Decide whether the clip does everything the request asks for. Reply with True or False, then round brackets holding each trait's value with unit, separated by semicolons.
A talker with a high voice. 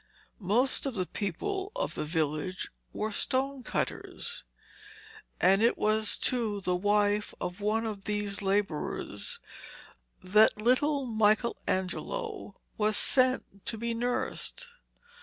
True (215 Hz)